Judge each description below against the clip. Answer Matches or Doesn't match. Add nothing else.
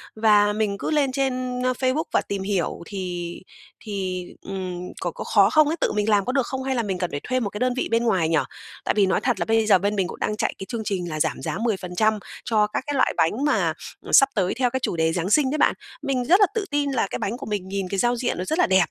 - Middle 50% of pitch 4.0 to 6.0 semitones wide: Matches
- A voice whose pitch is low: Doesn't match